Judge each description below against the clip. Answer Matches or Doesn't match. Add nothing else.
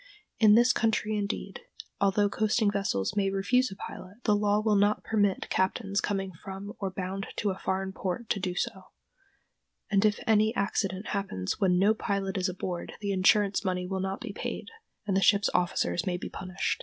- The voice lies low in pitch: Doesn't match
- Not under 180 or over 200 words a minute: Matches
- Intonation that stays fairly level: Matches